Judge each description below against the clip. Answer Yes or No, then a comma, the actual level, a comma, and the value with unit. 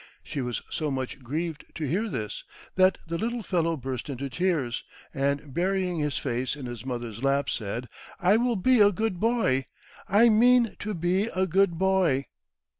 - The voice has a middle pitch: Yes, medium, 165 Hz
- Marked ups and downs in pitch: Yes, wide, 6.6 semitones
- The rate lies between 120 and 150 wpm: No, average, 175 wpm